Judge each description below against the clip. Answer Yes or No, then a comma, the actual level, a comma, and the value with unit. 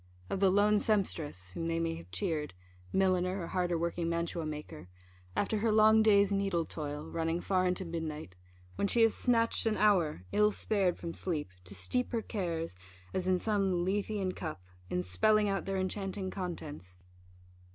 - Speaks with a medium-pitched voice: Yes, medium, 180 Hz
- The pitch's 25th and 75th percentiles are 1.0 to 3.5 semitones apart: No, average, 3.9 semitones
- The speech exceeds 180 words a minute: No, average, 170 wpm